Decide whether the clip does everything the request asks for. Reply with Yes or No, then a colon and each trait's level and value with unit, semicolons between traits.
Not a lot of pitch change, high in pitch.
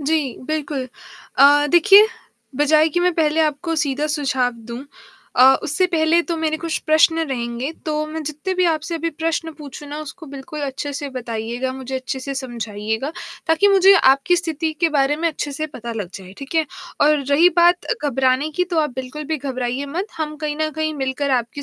No: average, 3.4 semitones; very high, 295 Hz